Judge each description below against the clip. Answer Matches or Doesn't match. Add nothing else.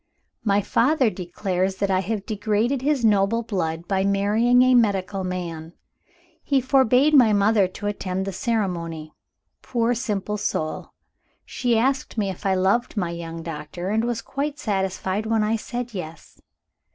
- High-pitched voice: Matches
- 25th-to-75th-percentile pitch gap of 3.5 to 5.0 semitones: Matches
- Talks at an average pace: Matches